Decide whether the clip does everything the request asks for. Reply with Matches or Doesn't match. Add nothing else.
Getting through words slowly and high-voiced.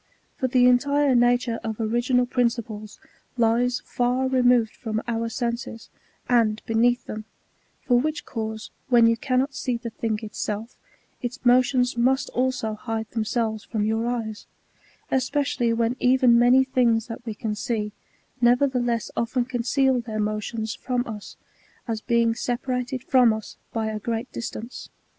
Doesn't match